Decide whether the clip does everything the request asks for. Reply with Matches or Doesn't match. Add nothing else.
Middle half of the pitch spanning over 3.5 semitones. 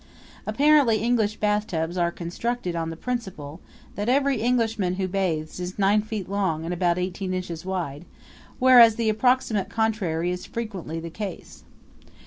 Matches